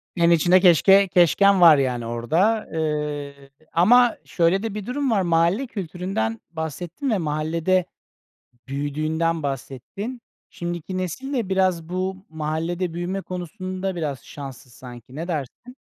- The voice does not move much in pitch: No, average, 4.0 semitones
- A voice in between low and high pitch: Yes, medium, 170 Hz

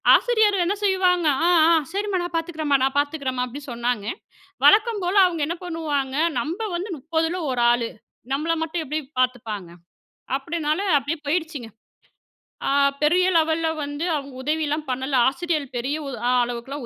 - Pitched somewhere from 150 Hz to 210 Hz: No, very high, 310 Hz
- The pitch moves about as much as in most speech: Yes, average, 4.4 semitones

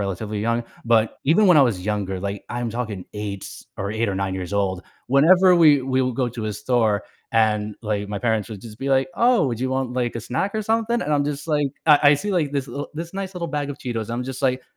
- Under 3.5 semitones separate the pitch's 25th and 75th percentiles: No, wide, 5.5 semitones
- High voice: No, low, 125 Hz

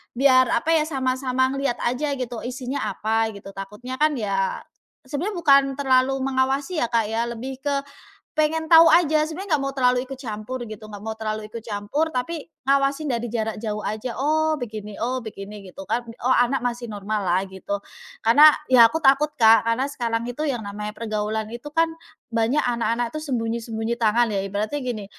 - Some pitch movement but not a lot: Yes, average, 4.0 semitones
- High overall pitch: Yes, high, 245 Hz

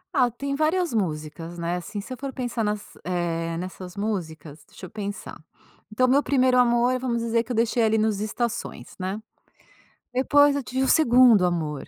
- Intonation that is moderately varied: No, wide, 6.0 semitones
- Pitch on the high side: Yes, high, 220 Hz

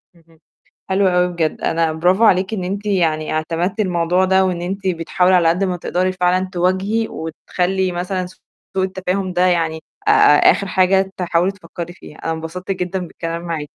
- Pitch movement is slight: Yes, narrow, 2.1 semitones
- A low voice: No, medium, 180 Hz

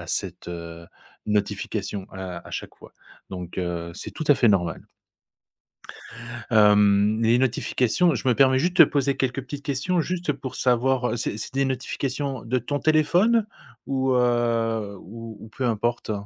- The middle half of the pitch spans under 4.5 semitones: No, average, 4.8 semitones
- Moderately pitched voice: No, low, 120 Hz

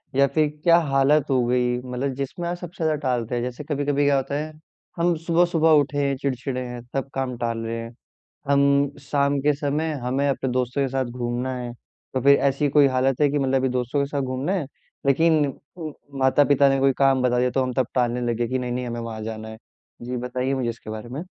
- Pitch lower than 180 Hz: Yes, low, 135 Hz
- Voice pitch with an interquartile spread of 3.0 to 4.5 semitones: No, narrow, 2.4 semitones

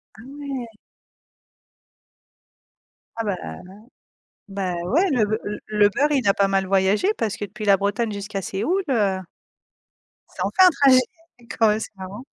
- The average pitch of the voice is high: Yes, high, 210 Hz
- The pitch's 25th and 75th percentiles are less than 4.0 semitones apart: No, average, 4.5 semitones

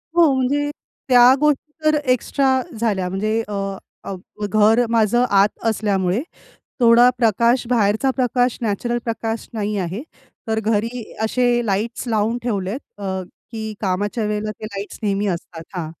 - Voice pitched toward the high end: Yes, high, 220 Hz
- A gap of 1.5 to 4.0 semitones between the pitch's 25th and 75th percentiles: Yes, average, 2.9 semitones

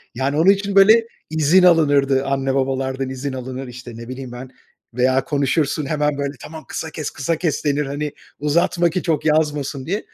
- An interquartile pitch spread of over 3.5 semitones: No, average, 3.2 semitones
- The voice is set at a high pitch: No, medium, 145 Hz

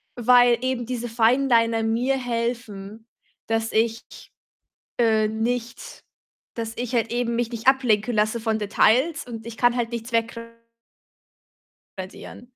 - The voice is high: Yes, high, 230 Hz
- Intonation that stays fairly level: Yes, narrow, 1.5 semitones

